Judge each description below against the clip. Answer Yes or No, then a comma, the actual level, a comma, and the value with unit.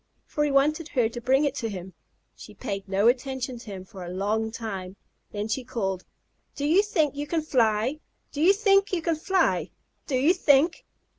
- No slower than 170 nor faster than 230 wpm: Yes, average, 200 wpm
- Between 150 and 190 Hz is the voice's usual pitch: No, very high, 260 Hz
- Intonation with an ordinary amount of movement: No, wide, 6.4 semitones